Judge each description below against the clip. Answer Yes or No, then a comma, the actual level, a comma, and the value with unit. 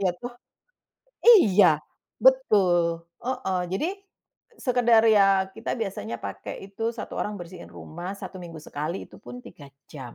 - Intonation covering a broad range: Yes, wide, 6.1 semitones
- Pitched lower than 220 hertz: Yes, high, 190 Hz